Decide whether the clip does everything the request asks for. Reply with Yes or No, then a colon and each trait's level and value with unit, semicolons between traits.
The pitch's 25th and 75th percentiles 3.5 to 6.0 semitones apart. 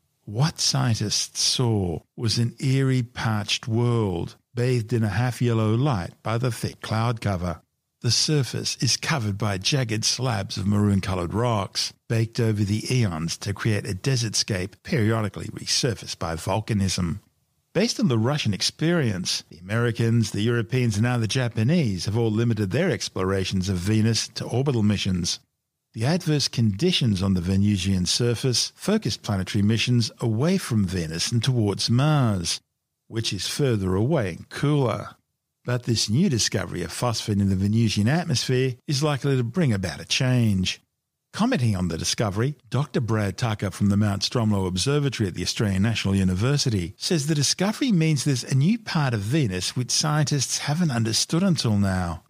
Yes: average, 4.2 semitones